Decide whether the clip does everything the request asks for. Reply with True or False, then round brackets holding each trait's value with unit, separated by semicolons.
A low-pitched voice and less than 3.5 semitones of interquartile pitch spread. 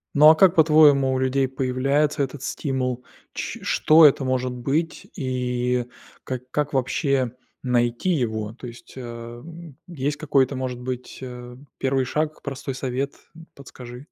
True (130 Hz; 2.4 semitones)